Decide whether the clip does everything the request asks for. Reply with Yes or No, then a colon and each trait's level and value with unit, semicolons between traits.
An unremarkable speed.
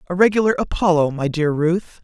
Yes: average, 175 wpm